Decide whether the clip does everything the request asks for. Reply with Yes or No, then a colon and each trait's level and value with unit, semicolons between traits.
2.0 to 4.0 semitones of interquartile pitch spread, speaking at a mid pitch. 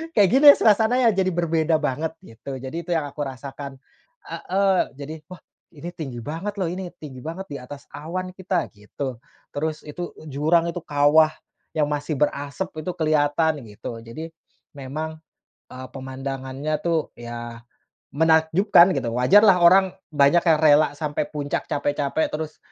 Yes: average, 3.5 semitones; medium, 155 Hz